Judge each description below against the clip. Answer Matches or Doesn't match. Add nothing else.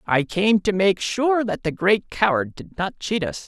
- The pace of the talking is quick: Matches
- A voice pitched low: Doesn't match